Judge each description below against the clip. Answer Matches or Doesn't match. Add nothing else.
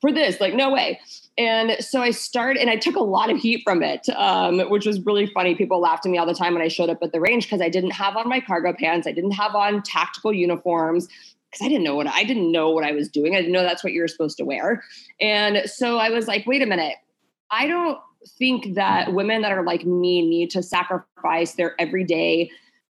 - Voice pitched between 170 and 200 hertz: Matches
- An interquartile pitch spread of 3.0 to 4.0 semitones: Doesn't match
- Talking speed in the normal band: Doesn't match